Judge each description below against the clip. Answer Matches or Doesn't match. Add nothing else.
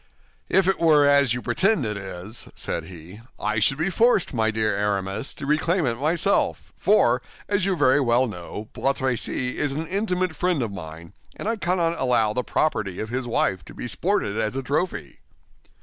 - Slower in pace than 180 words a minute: Doesn't match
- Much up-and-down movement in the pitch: Matches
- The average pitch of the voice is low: Matches